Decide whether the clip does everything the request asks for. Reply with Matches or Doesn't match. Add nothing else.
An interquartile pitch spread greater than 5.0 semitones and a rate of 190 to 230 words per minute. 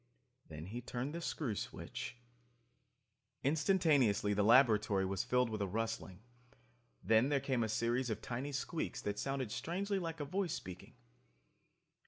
Doesn't match